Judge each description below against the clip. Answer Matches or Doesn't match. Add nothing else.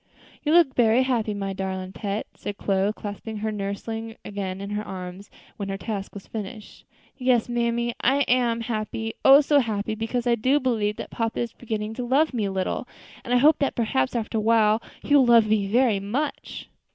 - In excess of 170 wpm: Matches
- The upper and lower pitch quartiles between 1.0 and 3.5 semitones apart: Matches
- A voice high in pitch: Matches